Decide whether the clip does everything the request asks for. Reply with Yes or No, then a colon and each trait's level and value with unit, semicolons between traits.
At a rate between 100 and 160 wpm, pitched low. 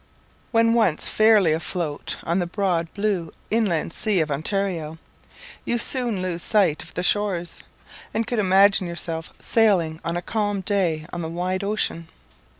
No: average, 150 wpm; medium, 185 Hz